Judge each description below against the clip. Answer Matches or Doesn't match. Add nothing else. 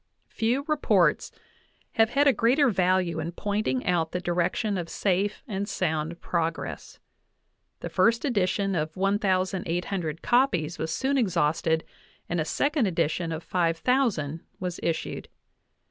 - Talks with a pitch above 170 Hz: Matches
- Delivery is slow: Matches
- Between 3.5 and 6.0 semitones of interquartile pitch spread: Matches